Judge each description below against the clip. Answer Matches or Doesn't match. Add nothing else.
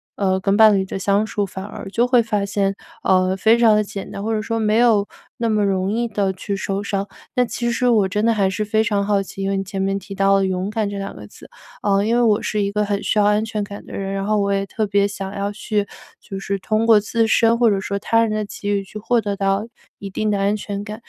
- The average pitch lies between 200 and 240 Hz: Matches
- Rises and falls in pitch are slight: Matches